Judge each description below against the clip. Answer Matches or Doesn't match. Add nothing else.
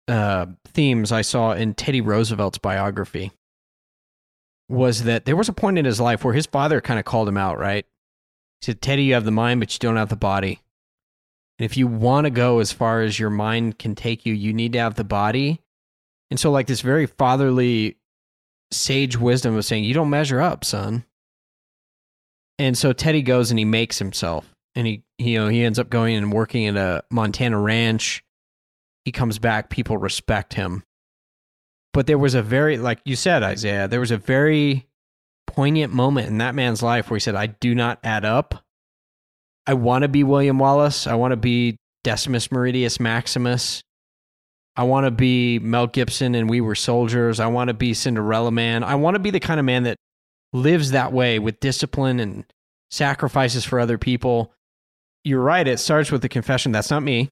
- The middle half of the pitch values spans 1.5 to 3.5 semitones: Matches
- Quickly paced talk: Doesn't match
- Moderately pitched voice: Doesn't match